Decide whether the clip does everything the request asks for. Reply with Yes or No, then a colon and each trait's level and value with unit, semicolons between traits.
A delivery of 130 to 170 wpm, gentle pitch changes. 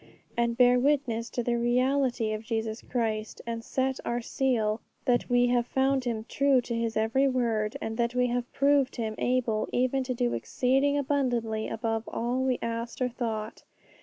No: average, 180 wpm; narrow, 2.2 semitones